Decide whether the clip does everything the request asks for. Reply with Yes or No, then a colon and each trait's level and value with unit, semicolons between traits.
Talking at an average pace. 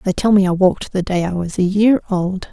No: fast, 285 wpm